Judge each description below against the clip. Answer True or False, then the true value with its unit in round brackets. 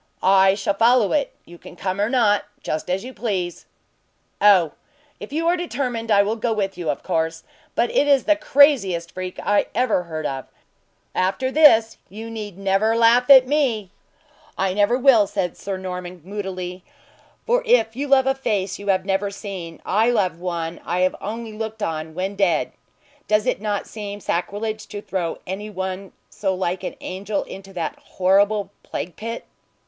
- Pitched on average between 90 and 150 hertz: False (200 Hz)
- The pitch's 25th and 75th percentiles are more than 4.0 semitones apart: False (3.7 semitones)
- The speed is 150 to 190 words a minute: True (175 wpm)